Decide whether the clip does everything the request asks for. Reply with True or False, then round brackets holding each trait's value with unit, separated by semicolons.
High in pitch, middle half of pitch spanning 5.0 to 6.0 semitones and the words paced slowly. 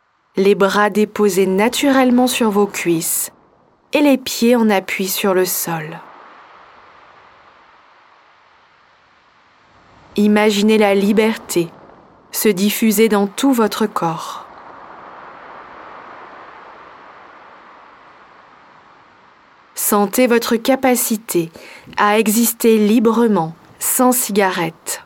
False (210 Hz; 3.5 semitones; 75 wpm)